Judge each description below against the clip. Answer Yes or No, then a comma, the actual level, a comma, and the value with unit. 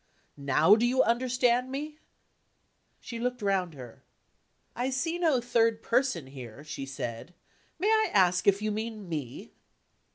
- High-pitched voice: Yes, high, 225 Hz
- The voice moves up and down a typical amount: No, wide, 6.9 semitones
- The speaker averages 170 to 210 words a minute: No, average, 140 wpm